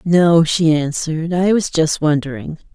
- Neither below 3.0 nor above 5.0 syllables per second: Yes, 4.4 syllables/s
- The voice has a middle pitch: Yes, medium, 160 Hz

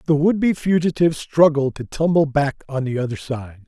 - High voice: No, medium, 145 Hz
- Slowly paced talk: No, average, 195 wpm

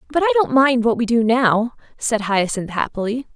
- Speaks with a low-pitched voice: No, high, 240 Hz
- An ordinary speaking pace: Yes, average, 195 wpm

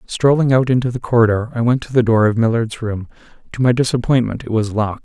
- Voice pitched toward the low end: Yes, low, 120 Hz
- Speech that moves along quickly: Yes, fast, 225 wpm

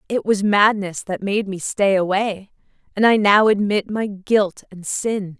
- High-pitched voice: Yes, high, 200 Hz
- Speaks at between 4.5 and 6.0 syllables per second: No, 4.0 syllables/s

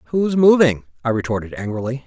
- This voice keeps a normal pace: Yes, average, 145 wpm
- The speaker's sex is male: Yes, male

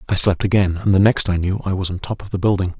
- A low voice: Yes, very low, 95 Hz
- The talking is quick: Yes, fast, 320 wpm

